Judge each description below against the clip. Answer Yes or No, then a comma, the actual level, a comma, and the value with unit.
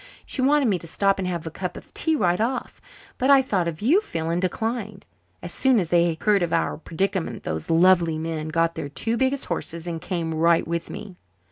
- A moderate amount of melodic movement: Yes, average, 5.0 semitones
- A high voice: No, medium, 175 Hz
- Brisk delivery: Yes, fast, 220 wpm